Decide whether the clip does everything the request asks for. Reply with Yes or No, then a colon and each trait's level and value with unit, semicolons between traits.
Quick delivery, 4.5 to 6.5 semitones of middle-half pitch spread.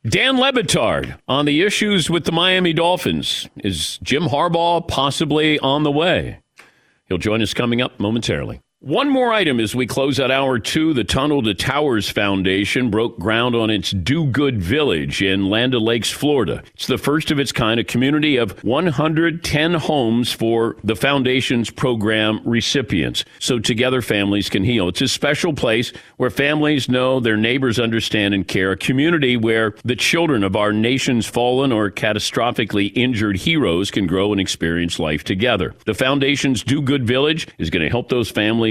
No: average, 170 wpm; average, 4.9 semitones